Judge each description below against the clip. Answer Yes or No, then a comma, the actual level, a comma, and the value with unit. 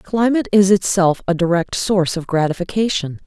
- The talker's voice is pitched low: No, medium, 185 Hz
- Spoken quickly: No, average, 145 wpm